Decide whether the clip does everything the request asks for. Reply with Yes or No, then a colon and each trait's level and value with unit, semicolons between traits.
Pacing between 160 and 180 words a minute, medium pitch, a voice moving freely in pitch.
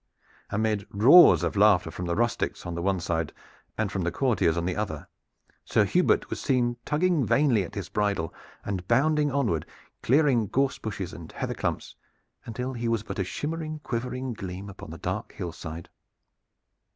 No: average, 170 wpm; low, 105 Hz; wide, 6.1 semitones